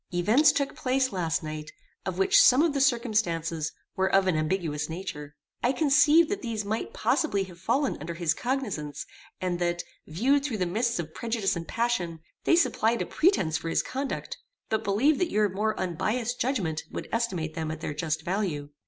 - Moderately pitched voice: No, high, 195 Hz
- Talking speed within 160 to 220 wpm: Yes, average, 185 wpm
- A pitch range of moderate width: No, wide, 7.0 semitones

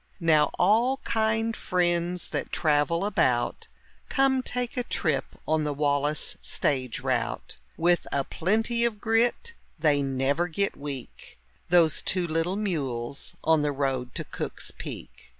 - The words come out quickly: No, slow, 135 wpm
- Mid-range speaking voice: Yes, medium, 165 Hz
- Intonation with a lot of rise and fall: Yes, wide, 6.8 semitones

